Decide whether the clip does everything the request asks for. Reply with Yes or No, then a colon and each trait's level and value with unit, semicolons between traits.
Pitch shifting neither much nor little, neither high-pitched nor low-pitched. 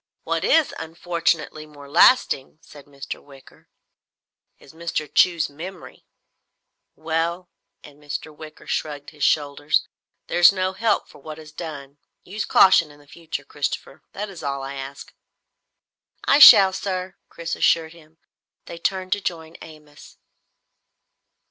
Yes: average, 3.3 semitones; medium, 160 Hz